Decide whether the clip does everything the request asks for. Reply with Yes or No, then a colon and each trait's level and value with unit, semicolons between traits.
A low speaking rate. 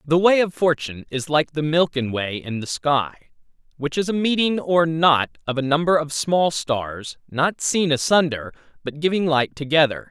No: average, 185 wpm